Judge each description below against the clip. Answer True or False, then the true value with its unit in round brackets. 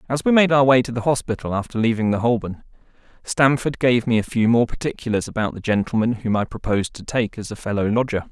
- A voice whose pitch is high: False (120 Hz)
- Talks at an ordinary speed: False (225 wpm)